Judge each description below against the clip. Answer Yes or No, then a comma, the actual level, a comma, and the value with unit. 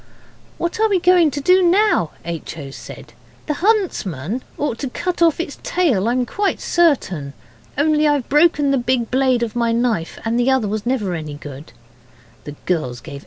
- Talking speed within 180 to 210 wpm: Yes, average, 185 wpm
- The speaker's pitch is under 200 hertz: No, very high, 255 Hz